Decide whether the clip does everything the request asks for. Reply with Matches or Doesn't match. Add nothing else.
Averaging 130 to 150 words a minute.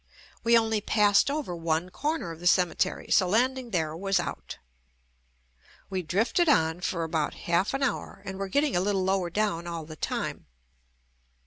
Doesn't match